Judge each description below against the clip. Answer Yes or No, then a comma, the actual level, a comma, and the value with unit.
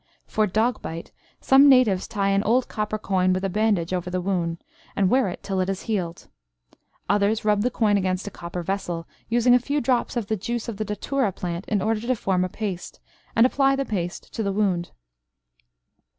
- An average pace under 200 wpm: No, fast, 205 wpm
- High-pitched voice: Yes, high, 205 Hz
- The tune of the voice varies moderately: Yes, average, 3.7 semitones